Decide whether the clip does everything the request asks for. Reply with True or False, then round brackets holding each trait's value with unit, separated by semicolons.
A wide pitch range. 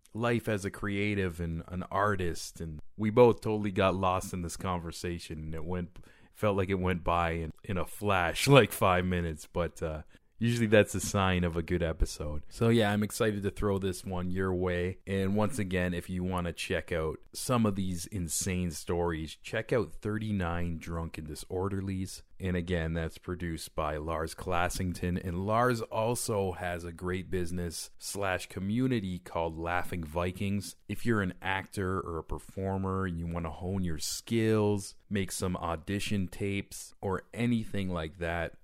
False (2.8 semitones)